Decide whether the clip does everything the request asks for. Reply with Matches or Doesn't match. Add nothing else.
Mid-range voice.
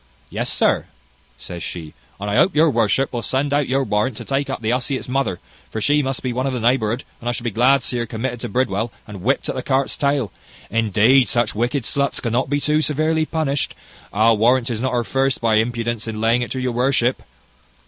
Doesn't match